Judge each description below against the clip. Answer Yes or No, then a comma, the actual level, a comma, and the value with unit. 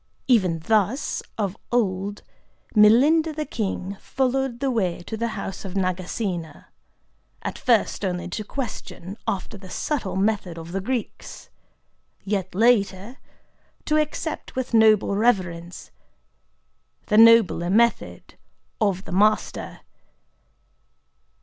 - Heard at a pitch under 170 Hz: No, high, 210 Hz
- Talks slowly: Yes, slow, 110 wpm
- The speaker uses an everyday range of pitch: Yes, average, 4.1 semitones